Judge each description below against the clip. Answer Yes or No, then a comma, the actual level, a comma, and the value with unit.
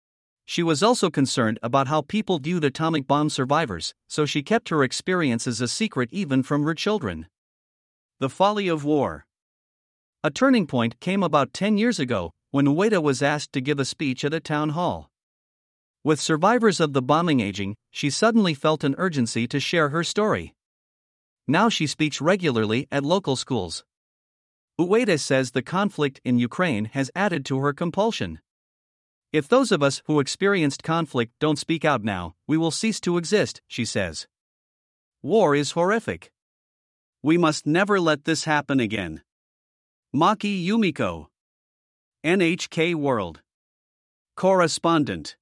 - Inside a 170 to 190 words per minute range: No, average, 150 wpm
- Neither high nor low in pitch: Yes, medium, 150 Hz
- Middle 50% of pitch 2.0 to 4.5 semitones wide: No, average, 5.1 semitones